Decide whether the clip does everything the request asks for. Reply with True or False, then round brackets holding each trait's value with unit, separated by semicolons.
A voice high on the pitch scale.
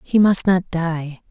False (175 Hz)